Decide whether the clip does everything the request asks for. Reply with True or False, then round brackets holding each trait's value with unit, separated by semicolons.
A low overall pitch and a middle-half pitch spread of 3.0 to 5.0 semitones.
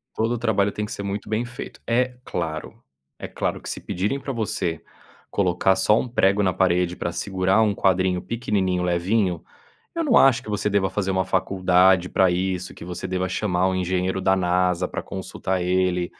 False (95 Hz; 2.4 semitones)